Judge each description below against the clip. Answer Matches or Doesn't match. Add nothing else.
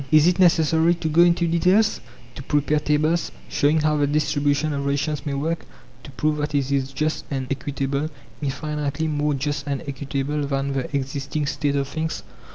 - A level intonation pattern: Matches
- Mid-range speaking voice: Matches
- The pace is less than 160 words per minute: Doesn't match